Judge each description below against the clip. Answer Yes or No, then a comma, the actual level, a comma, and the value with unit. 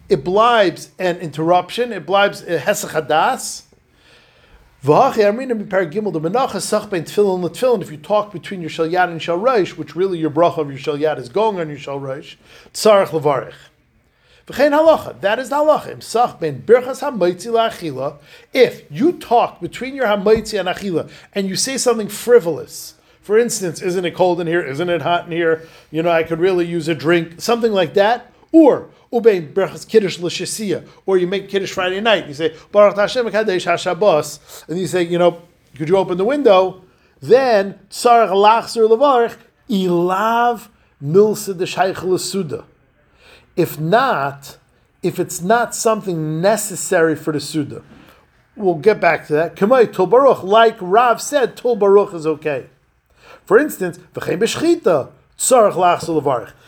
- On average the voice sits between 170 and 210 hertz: Yes, medium, 185 Hz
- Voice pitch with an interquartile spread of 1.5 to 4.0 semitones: No, average, 5.0 semitones